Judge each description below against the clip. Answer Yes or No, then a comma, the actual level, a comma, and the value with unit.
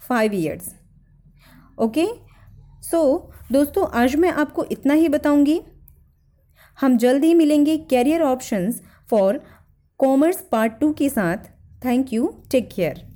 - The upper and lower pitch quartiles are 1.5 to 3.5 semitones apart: No, average, 4.7 semitones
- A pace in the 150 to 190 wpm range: No, average, 125 wpm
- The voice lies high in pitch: Yes, very high, 280 Hz